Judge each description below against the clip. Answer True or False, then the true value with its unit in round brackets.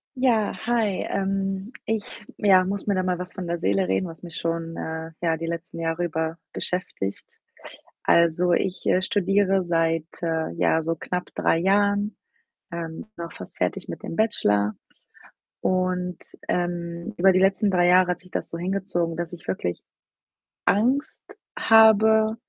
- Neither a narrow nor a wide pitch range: True (3.0 semitones)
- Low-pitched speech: False (180 Hz)